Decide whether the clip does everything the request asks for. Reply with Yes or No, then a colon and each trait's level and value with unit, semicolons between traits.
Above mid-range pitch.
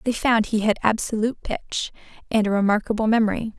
Yes: high, 215 Hz